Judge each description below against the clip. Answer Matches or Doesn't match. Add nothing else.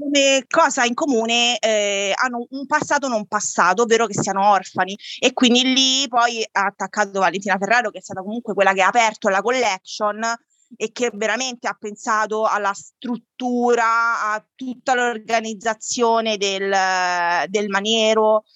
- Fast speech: Doesn't match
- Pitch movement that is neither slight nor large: Matches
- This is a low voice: Doesn't match